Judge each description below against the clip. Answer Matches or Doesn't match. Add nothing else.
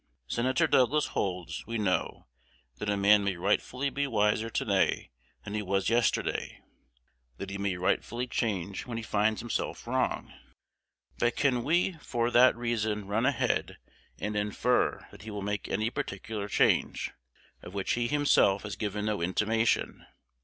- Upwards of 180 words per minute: Doesn't match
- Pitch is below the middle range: Matches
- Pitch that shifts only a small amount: Doesn't match